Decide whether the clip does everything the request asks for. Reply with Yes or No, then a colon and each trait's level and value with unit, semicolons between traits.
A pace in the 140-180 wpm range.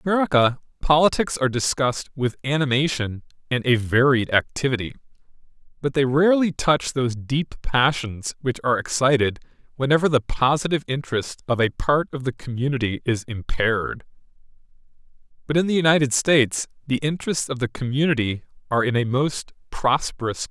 Yes: average, 145 wpm